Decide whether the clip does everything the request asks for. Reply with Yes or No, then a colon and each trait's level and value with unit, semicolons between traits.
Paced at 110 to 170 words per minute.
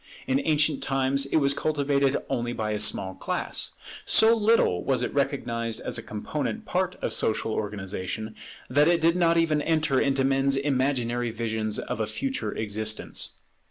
Yes: average, 160 wpm